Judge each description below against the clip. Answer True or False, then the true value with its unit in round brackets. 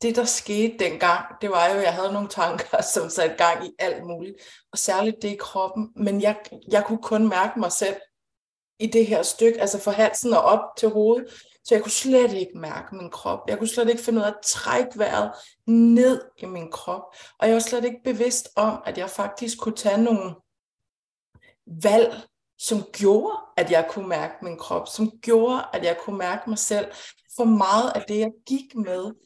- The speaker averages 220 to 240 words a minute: False (205 wpm)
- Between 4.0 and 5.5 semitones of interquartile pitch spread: False (3.3 semitones)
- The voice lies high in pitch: True (210 Hz)